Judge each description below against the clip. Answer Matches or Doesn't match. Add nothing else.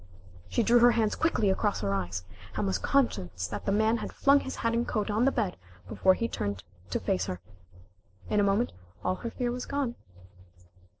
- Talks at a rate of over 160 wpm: Matches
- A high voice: Matches